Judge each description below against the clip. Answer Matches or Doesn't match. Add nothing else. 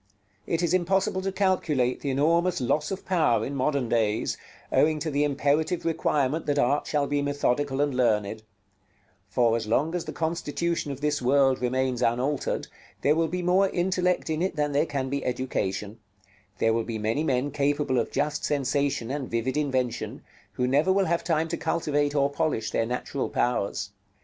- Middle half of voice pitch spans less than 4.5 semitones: Matches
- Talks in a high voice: Doesn't match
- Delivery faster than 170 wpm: Matches